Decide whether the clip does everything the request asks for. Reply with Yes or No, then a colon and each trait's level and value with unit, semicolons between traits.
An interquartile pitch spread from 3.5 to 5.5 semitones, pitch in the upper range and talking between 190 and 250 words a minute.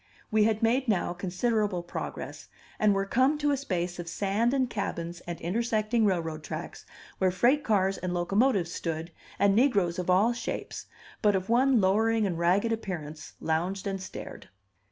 No: average, 4.4 semitones; high, 195 Hz; average, 165 wpm